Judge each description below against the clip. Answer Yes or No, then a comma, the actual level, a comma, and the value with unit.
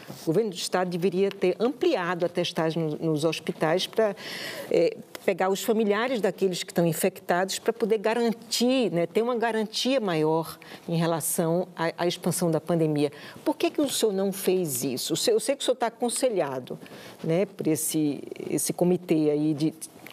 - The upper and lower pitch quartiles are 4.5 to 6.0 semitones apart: Yes, average, 5.1 semitones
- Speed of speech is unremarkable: Yes, average, 175 wpm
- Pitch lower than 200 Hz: Yes, medium, 185 Hz